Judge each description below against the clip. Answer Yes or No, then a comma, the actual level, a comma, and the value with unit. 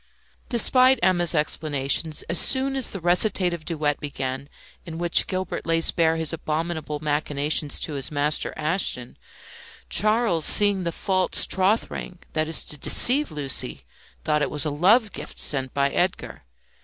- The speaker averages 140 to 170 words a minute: Yes, average, 150 wpm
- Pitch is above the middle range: No, medium, 160 Hz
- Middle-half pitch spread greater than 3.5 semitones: Yes, average, 4.1 semitones